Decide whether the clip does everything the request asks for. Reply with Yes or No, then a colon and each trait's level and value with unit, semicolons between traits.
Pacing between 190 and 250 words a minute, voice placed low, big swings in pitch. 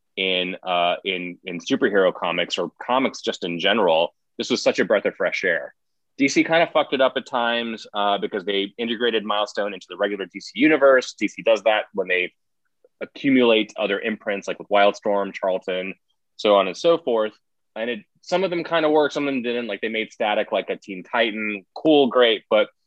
Yes: average, 200 wpm; low, 115 Hz; wide, 7.3 semitones